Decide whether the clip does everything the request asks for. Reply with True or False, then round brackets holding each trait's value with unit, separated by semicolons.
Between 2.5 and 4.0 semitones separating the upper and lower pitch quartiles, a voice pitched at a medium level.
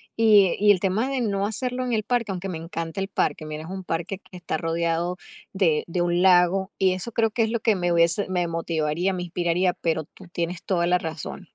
True (3.0 semitones; 180 Hz)